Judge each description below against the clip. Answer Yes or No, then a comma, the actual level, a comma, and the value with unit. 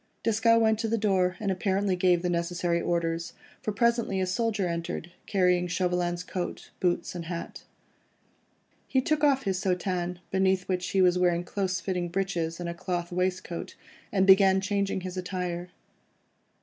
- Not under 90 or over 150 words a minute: No, average, 160 wpm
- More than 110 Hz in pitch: Yes, medium, 185 Hz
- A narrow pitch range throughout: Yes, narrow, 1.9 semitones